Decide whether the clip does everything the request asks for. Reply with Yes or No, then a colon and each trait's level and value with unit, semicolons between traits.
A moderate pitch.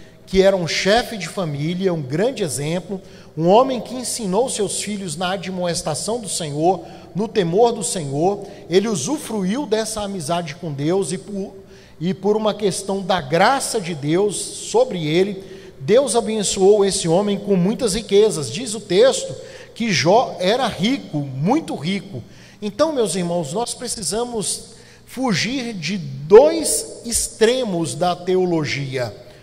No: high, 195 Hz